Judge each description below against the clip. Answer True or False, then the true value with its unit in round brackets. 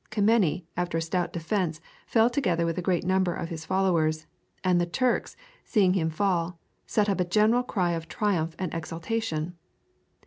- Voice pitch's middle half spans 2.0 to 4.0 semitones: True (3.5 semitones)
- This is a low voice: False (180 Hz)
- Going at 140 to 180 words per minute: True (170 wpm)